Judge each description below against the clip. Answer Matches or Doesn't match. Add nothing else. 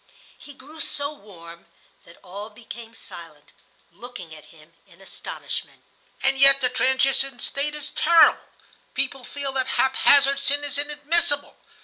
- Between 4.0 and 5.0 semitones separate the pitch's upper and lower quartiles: Doesn't match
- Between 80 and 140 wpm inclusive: Matches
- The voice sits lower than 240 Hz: Doesn't match